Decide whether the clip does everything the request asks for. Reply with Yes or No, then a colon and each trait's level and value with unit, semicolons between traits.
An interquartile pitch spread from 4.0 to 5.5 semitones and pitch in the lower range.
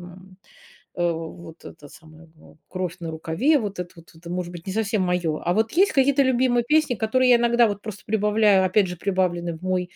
No: average, 4.7 semitones; medium, 185 Hz